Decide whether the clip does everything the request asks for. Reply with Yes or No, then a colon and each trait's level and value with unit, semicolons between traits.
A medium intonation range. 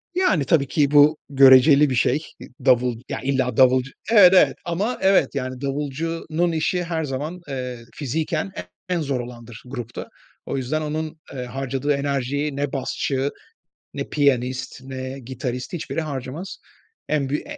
Yes: average, 3.2 semitones